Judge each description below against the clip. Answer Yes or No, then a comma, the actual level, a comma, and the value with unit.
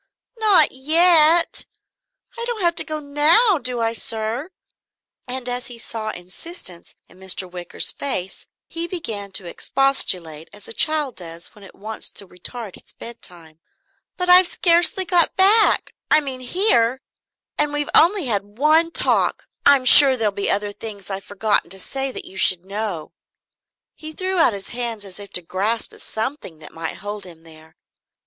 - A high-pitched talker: Yes, high, 235 Hz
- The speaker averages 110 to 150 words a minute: No, average, 170 wpm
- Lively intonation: Yes, wide, 8.1 semitones